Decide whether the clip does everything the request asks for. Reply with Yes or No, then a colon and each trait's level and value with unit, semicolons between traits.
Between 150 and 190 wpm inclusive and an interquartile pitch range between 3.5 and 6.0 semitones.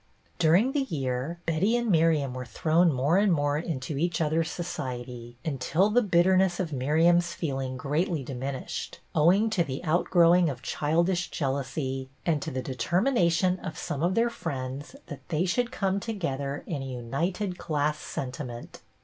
Yes: average, 160 wpm; average, 4.8 semitones